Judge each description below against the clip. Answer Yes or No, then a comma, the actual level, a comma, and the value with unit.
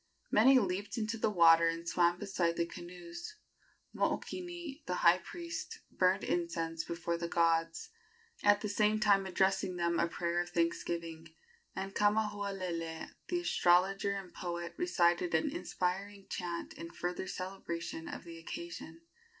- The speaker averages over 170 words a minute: No, average, 140 wpm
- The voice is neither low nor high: Yes, medium, 180 Hz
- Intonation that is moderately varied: Yes, average, 3.2 semitones